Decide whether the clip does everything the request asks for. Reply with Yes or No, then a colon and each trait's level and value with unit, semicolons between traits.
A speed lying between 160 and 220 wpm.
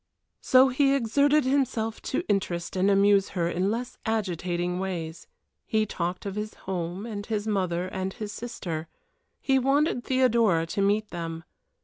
No: average, 150 wpm